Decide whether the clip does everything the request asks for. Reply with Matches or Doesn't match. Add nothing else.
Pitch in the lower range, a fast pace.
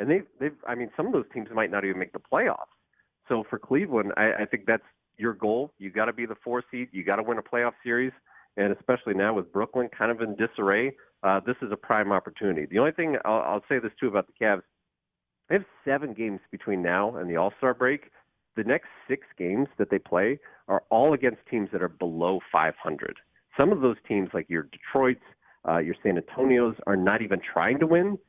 Matches